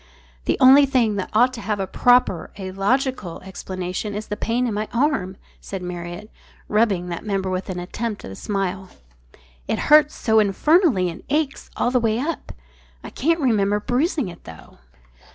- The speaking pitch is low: No, high, 210 Hz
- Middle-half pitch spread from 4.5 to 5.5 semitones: Yes, average, 5.1 semitones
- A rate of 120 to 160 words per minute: No, average, 175 wpm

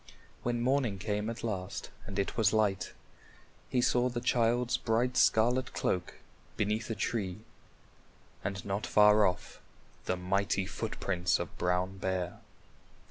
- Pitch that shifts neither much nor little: Yes, average, 3.8 semitones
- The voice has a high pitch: No, low, 105 Hz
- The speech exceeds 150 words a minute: No, slow, 135 wpm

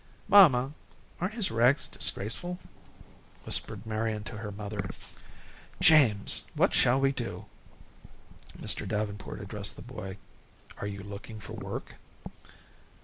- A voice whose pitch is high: No, low, 110 Hz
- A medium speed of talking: No, slow, 115 wpm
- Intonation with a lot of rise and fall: No, average, 4.7 semitones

